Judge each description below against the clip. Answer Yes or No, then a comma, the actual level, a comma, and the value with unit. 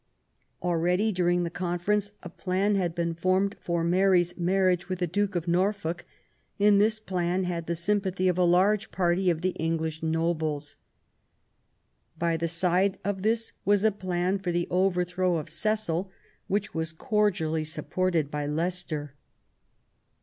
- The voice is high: No, medium, 180 Hz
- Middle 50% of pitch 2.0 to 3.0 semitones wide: Yes, narrow, 2.4 semitones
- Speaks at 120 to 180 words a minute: Yes, average, 150 wpm